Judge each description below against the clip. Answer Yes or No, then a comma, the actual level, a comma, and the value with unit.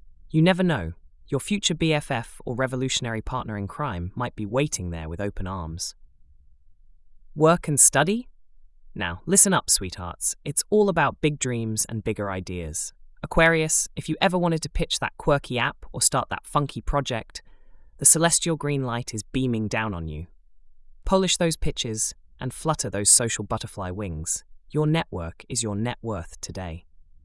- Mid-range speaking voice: No, low, 115 Hz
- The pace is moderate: Yes, average, 165 wpm